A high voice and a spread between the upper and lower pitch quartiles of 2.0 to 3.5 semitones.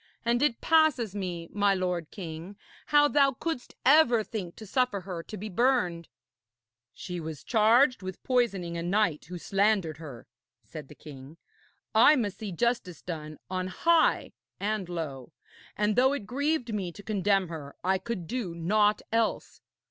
No: high, 200 Hz; wide, 5.6 semitones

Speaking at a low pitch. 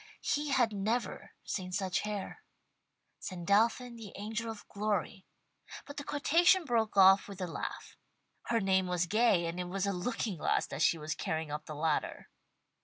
No: high, 200 Hz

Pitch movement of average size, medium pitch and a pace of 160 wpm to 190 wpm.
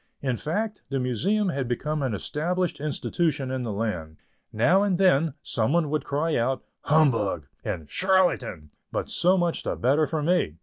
No: wide, 6.2 semitones; medium, 150 Hz; average, 170 wpm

